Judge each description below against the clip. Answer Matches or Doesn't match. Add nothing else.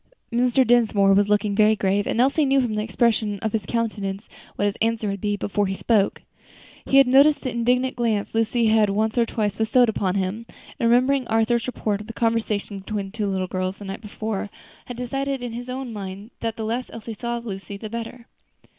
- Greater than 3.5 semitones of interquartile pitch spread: Doesn't match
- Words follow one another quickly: Matches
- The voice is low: Doesn't match